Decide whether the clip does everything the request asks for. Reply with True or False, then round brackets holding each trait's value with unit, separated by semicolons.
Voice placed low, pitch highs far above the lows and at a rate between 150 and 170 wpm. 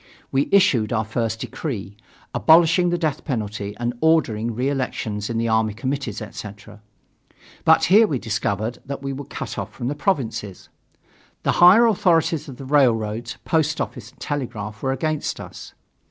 True (125 Hz; 5.7 semitones; 155 wpm)